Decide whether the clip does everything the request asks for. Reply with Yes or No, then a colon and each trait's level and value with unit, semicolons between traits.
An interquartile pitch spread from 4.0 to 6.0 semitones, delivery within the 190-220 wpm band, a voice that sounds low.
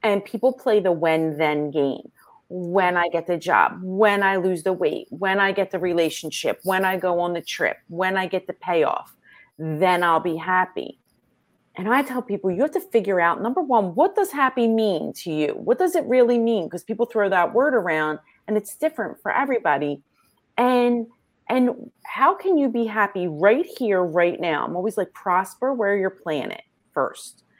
No: average, 5.2 semitones; average, 195 wpm; high, 195 Hz